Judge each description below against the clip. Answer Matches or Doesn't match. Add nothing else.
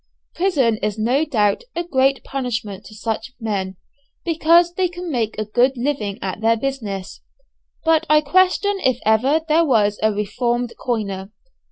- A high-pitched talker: Matches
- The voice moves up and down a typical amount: Doesn't match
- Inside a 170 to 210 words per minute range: Doesn't match